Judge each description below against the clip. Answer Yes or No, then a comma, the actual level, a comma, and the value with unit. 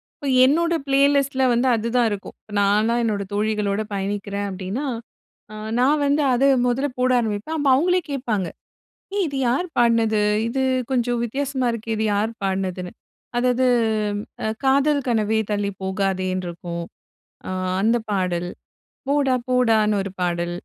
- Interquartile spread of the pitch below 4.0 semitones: No, average, 4.8 semitones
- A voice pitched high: Yes, high, 225 Hz